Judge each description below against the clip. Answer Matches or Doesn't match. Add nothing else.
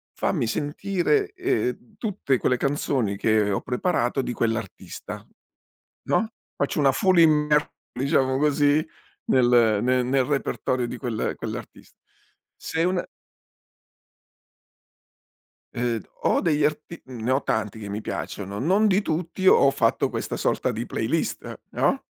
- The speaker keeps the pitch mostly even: Doesn't match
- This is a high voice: Doesn't match